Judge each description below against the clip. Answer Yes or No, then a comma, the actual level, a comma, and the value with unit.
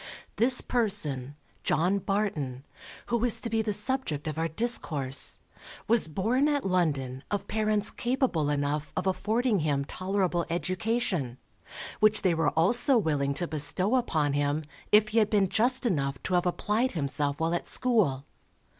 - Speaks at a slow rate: No, average, 155 wpm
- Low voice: No, medium, 185 Hz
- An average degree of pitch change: No, wide, 6.9 semitones